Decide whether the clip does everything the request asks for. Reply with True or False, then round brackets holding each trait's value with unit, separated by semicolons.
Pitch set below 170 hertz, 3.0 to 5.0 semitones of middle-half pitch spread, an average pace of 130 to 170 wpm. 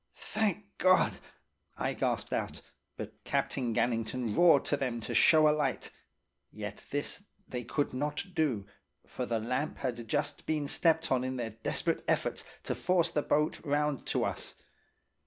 True (140 Hz; 4.6 semitones; 155 wpm)